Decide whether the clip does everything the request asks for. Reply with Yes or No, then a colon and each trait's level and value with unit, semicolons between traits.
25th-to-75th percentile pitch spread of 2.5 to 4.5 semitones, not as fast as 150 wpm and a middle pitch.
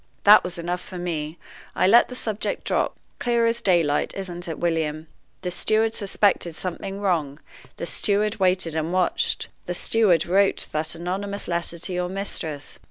No: average, 3.1 semitones; average, 165 wpm; medium, 180 Hz